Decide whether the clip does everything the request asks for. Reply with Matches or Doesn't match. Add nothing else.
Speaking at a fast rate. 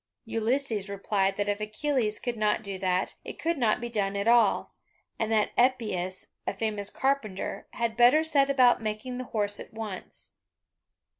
Doesn't match